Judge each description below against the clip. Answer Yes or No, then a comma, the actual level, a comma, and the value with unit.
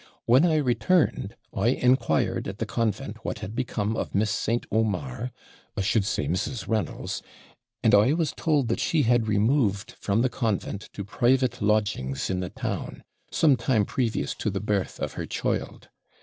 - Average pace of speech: Yes, average, 170 wpm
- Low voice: Yes, low, 110 Hz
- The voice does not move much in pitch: No, average, 3.9 semitones